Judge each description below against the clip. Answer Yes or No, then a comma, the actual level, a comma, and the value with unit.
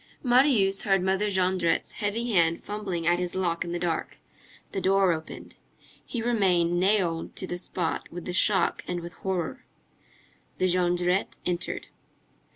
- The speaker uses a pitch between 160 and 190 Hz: Yes, medium, 185 Hz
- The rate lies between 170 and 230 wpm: No, average, 150 wpm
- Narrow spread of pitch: Yes, narrow, 2.1 semitones